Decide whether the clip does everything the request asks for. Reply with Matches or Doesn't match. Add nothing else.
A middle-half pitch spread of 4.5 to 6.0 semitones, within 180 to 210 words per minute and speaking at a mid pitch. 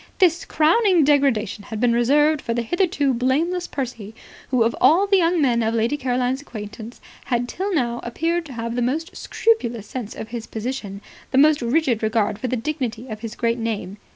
Doesn't match